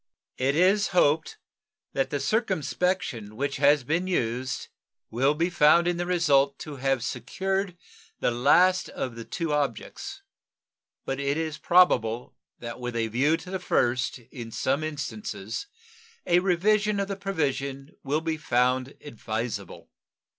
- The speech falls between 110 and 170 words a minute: Yes, average, 140 wpm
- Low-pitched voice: No, medium, 145 Hz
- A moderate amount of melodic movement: No, wide, 5.7 semitones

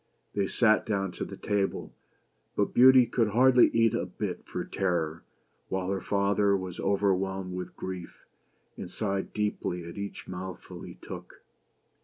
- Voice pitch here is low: Yes, low, 100 Hz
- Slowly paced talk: No, average, 145 wpm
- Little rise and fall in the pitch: Yes, narrow, 2.2 semitones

